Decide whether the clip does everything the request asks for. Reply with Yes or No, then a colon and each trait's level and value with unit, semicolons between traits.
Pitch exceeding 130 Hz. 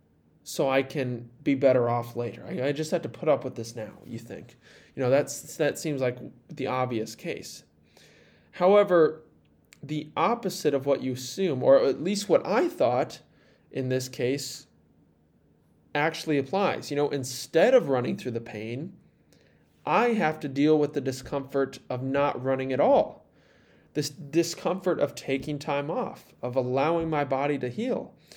Yes: medium, 140 Hz